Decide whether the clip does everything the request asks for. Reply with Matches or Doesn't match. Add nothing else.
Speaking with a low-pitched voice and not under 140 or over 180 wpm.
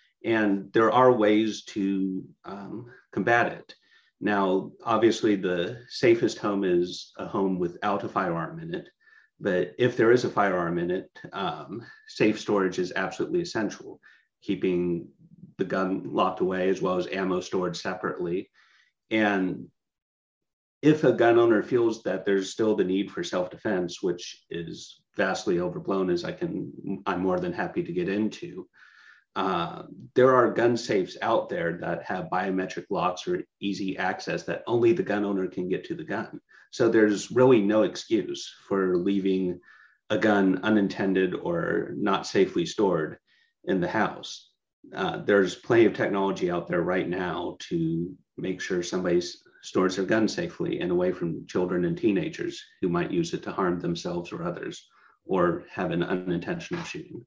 Matches